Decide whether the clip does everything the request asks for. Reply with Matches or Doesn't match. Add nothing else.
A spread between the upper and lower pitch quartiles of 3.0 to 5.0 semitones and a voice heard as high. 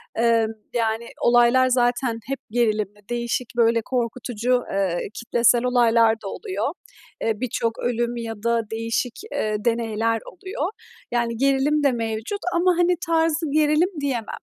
Doesn't match